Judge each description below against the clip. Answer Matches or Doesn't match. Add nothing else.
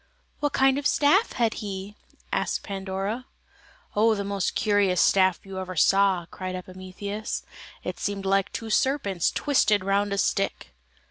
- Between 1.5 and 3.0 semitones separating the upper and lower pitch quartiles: Matches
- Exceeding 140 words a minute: Matches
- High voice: Matches